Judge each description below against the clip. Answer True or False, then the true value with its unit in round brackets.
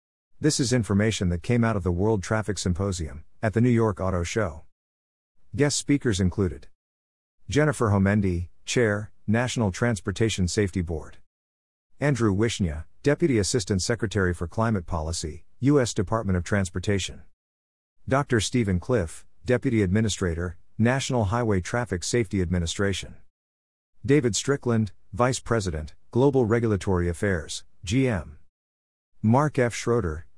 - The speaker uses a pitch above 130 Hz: False (100 Hz)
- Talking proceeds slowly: True (120 wpm)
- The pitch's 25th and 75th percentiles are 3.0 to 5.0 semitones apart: False (5.4 semitones)